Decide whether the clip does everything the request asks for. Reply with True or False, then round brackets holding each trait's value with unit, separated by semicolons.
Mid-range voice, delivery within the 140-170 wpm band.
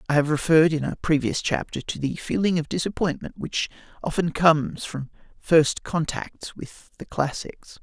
True (155 Hz; 160 wpm)